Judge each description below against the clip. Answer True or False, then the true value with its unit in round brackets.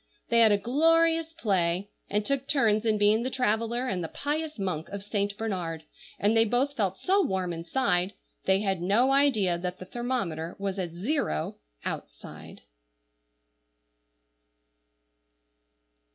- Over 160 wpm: False (140 wpm)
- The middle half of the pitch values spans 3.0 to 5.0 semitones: False (5.6 semitones)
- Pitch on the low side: False (210 Hz)